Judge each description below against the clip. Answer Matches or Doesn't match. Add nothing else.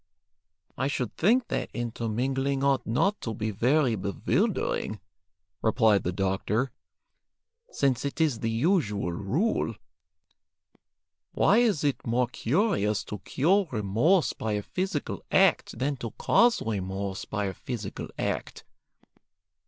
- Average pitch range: Doesn't match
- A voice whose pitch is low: Matches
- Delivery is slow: Matches